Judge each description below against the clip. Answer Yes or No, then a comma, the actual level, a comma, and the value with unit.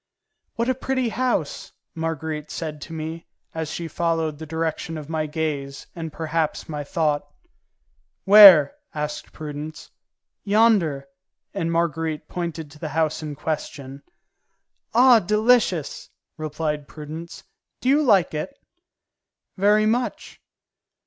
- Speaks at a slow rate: Yes, slow, 120 wpm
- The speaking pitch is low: No, medium, 160 Hz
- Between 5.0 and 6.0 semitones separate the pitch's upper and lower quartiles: No, average, 4.1 semitones